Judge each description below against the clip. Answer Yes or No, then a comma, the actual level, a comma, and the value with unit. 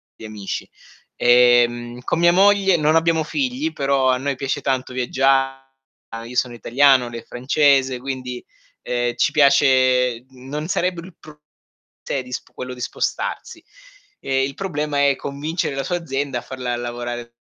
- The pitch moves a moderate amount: Yes, average, 3.3 semitones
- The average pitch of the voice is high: No, low, 135 Hz